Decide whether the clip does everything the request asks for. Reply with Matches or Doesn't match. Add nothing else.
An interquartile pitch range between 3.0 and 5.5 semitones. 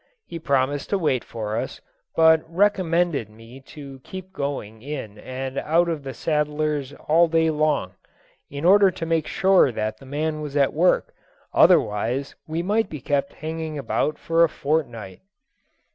Matches